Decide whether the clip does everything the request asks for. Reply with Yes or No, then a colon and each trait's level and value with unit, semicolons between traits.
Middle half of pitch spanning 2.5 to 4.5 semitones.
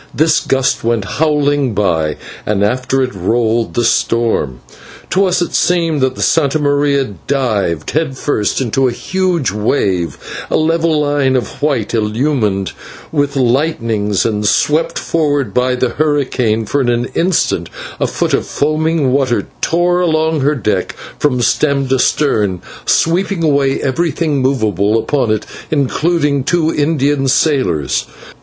No: average, 5.2 semitones